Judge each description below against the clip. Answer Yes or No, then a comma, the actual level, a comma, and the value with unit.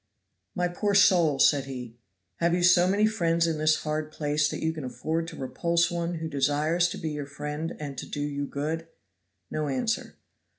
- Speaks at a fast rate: No, average, 195 wpm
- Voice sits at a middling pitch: Yes, medium, 155 Hz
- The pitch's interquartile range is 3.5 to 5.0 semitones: No, average, 2.7 semitones